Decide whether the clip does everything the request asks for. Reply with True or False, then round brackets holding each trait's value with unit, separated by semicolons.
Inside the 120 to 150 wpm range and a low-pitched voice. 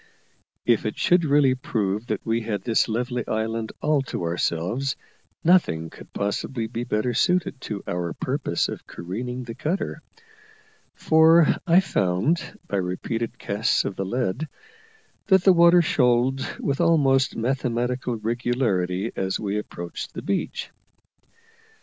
True (135 wpm; 120 Hz)